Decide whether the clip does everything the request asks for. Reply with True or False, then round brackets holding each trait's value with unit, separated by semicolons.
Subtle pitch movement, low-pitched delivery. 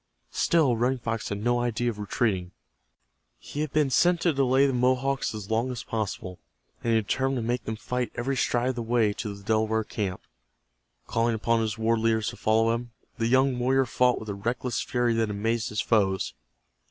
True (2.3 semitones; 115 Hz)